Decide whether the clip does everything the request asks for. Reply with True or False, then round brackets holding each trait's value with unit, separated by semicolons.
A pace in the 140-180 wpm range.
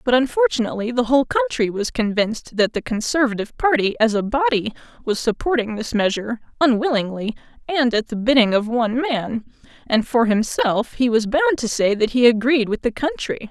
True (175 wpm)